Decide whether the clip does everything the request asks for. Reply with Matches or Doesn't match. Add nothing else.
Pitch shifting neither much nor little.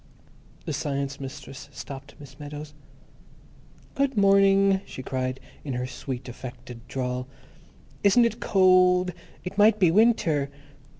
Doesn't match